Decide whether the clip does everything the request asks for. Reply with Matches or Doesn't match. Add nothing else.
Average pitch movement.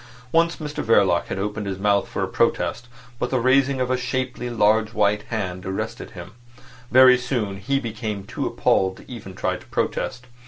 Matches